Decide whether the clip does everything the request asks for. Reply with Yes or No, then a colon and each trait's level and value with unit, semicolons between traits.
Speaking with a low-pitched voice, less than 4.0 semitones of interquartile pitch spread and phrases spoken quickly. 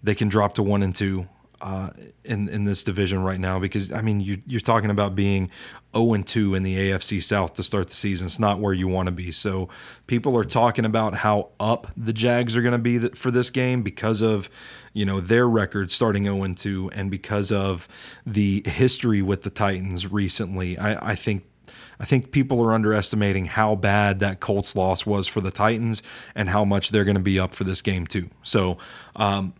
Yes: low, 100 Hz; narrow, 2.4 semitones; fast, 215 wpm